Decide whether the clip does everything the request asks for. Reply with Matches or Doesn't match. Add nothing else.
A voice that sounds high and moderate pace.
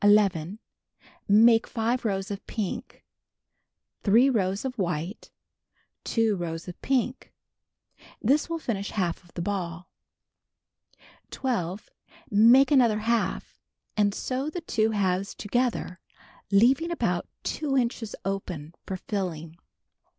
Doesn't match